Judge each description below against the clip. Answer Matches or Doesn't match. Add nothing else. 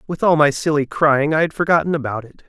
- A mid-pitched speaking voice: Matches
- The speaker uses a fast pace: Matches